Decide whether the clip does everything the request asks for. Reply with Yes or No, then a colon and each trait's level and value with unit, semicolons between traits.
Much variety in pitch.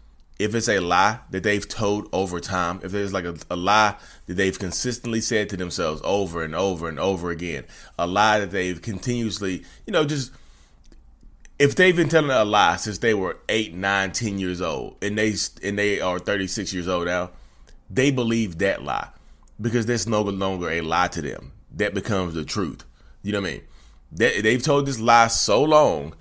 No: average, 4.1 semitones